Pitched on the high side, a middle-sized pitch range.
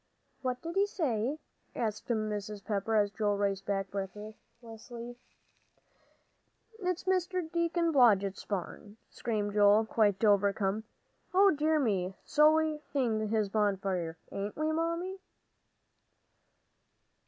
No: high, 220 Hz; wide, 7.0 semitones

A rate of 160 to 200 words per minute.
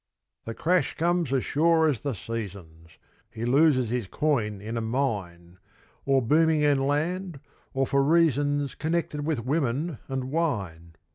No: average, 145 wpm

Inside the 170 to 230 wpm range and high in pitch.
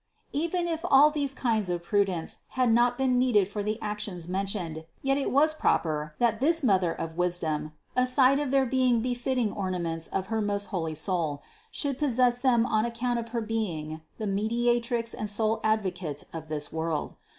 Yes: average, 175 wpm; high, 220 Hz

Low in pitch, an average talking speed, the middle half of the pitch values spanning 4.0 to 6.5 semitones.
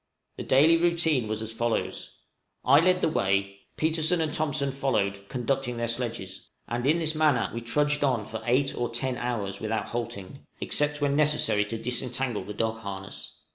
Yes: low, 125 Hz; average, 175 wpm; average, 4.9 semitones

